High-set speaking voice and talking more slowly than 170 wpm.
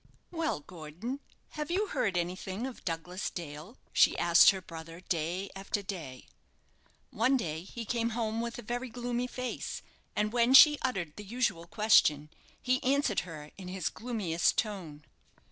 Yes: high, 200 Hz; average, 155 wpm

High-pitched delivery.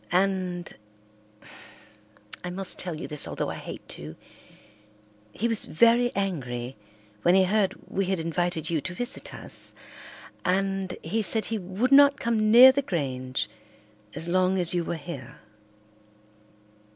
No: medium, 180 Hz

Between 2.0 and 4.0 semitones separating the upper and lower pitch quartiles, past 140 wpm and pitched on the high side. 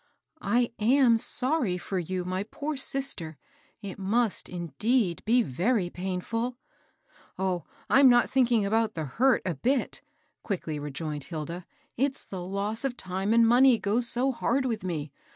No: wide, 5.4 semitones; average, 155 wpm; high, 210 Hz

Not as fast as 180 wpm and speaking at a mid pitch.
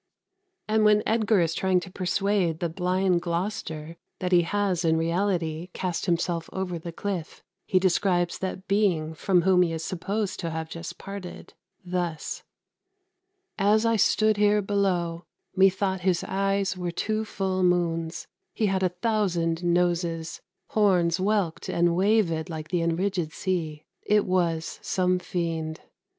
Yes: average, 145 wpm; medium, 180 Hz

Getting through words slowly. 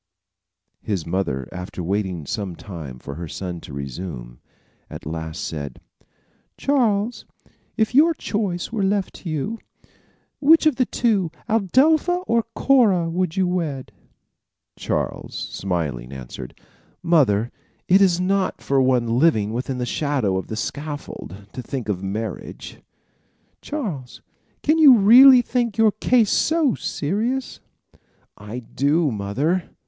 Yes: slow, 125 wpm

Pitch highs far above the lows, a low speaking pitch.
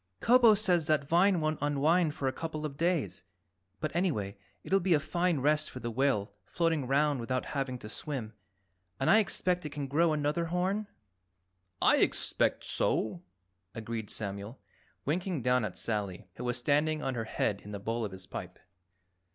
No: wide, 6.3 semitones; medium, 145 Hz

